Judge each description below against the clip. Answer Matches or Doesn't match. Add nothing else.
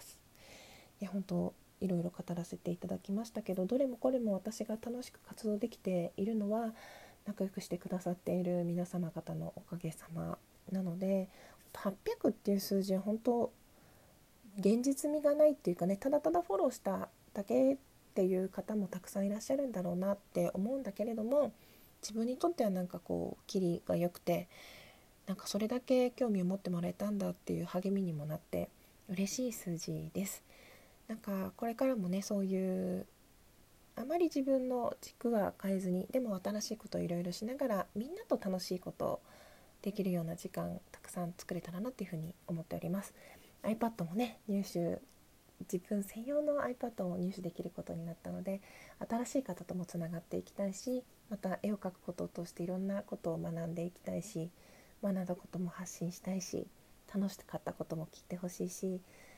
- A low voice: Doesn't match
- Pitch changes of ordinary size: Matches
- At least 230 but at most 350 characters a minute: Doesn't match